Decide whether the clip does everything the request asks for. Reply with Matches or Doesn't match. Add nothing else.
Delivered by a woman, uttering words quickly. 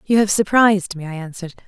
Matches